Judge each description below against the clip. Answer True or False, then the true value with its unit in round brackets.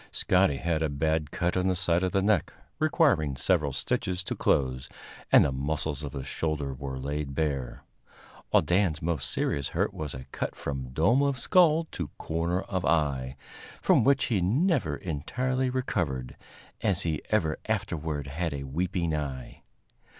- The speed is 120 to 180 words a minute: True (165 wpm)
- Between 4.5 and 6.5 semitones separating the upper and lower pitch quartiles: True (4.8 semitones)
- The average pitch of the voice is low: True (80 Hz)